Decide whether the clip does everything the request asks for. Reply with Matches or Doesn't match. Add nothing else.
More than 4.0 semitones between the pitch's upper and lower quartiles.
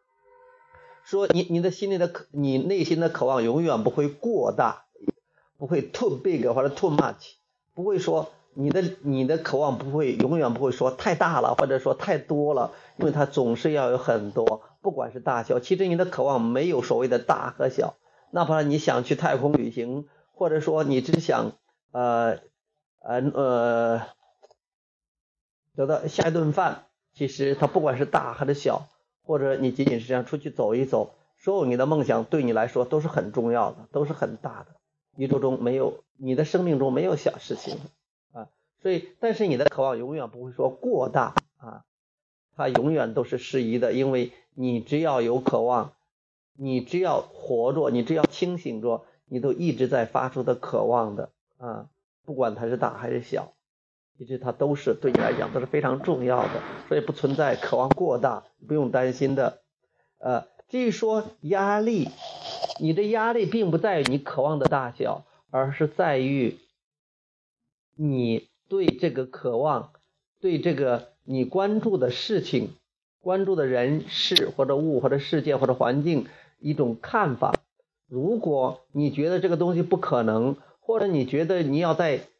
Matches